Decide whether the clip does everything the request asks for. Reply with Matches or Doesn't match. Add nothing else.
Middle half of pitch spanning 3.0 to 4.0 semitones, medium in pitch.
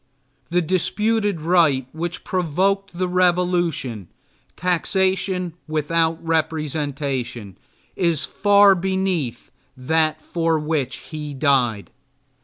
Matches